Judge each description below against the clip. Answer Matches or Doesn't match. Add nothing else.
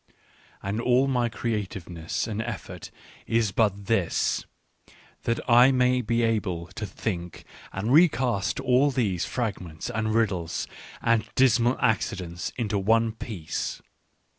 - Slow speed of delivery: Matches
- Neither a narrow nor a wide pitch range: Matches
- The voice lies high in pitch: Doesn't match